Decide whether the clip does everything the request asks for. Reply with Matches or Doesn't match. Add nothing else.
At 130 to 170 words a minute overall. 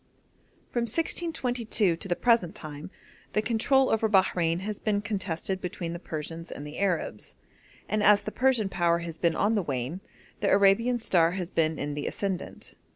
Matches